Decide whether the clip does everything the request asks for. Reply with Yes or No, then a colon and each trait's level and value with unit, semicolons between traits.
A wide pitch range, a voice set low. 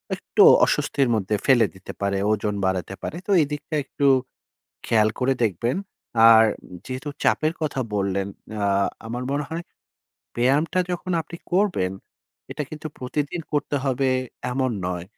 Yes: wide, 6.2 semitones; low, 130 Hz